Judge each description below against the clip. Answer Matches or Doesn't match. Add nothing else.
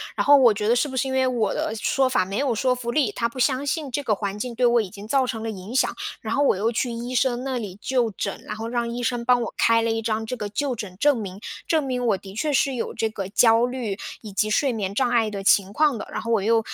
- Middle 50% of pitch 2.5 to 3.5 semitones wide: Matches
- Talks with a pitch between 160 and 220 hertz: Doesn't match